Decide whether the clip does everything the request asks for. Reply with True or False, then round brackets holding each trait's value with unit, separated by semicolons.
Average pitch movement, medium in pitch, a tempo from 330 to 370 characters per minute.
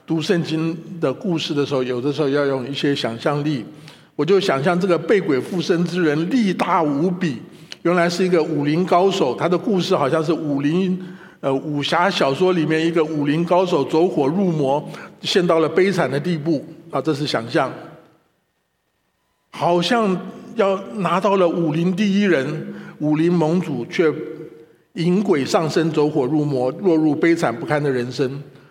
False (3.3 semitones; 165 Hz; 245 characters per minute)